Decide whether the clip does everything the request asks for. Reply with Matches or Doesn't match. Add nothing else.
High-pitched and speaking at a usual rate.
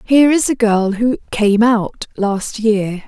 Matches